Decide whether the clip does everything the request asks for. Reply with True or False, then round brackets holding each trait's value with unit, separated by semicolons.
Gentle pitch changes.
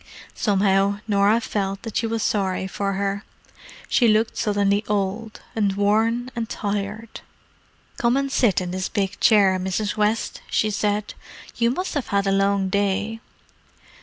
True (2.1 semitones)